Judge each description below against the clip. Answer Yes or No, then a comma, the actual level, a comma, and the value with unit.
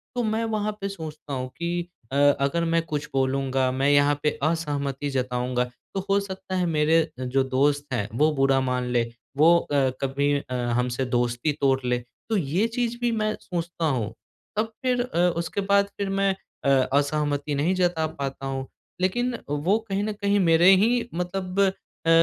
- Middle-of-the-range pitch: Yes, medium, 155 Hz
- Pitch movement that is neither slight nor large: No, wide, 6.3 semitones